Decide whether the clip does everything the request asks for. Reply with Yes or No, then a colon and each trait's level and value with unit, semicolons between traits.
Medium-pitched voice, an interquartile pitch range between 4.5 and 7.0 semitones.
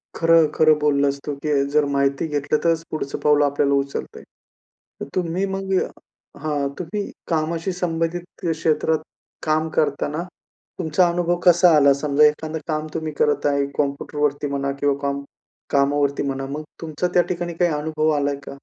No: medium, 150 Hz; narrow, 2.5 semitones